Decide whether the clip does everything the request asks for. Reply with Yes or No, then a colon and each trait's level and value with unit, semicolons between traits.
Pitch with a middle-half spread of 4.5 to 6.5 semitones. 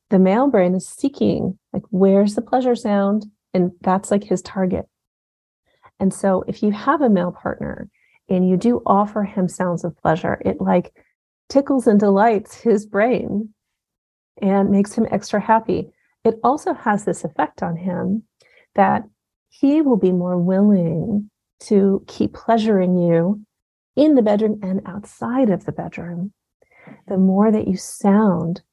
No: average, 3.3 semitones